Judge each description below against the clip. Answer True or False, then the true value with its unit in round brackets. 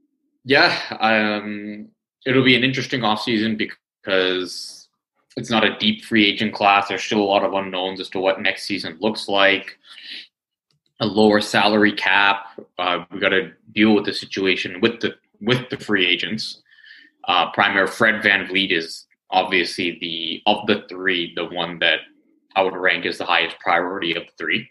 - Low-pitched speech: True (105 Hz)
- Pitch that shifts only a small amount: False (4.3 semitones)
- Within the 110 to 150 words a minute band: False (170 wpm)